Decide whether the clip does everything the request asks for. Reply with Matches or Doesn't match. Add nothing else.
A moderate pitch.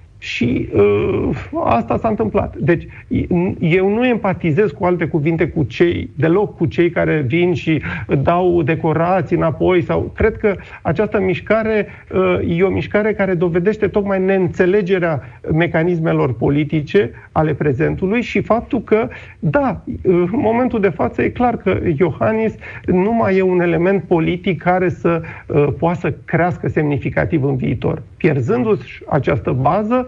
Matches